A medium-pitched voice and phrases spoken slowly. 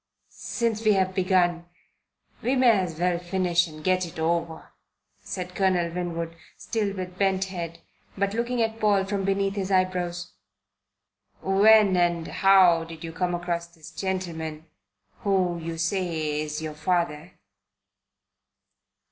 Yes: medium, 180 Hz; slow, 130 wpm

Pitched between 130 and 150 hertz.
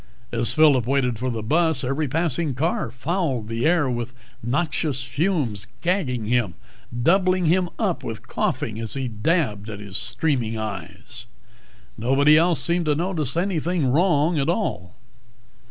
Yes: medium, 140 Hz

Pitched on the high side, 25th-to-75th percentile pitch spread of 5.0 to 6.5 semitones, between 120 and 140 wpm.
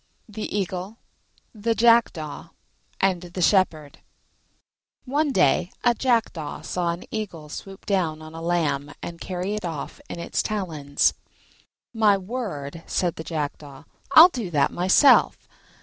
No: medium, 180 Hz; average, 5.3 semitones; slow, 135 wpm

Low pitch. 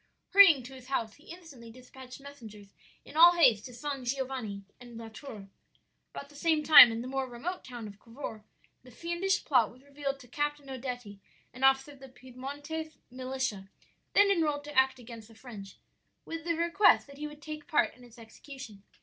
No: very high, 265 Hz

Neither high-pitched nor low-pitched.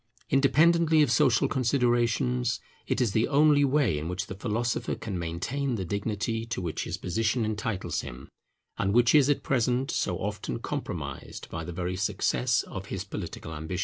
No: low, 115 Hz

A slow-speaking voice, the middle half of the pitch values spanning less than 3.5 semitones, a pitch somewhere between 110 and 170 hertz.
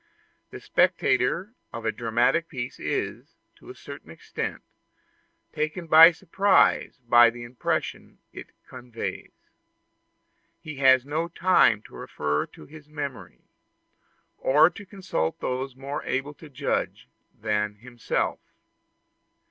No: slow, 115 wpm; wide, 5.4 semitones; low, 135 Hz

